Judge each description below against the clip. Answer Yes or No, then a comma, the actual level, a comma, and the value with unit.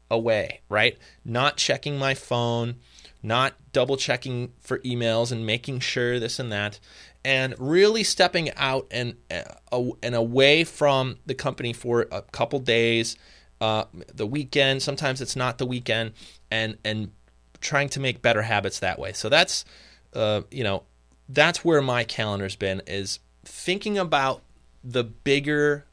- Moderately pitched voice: No, low, 120 Hz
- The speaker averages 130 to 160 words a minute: Yes, average, 150 wpm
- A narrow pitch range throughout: No, average, 4.3 semitones